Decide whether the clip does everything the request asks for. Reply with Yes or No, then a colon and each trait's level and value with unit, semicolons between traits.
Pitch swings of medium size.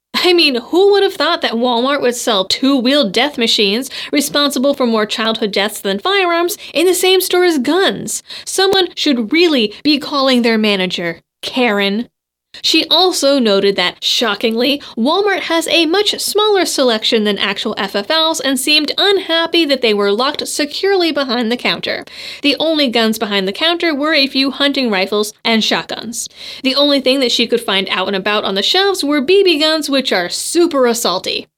No: wide, 6.5 semitones